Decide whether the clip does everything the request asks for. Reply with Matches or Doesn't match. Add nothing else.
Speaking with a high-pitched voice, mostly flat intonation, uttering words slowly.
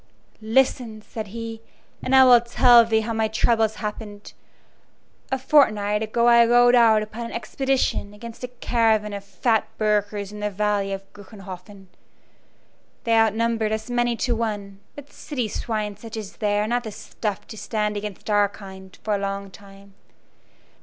Doesn't match